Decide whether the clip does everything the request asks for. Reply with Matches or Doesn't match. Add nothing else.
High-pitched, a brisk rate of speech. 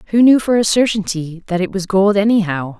Matches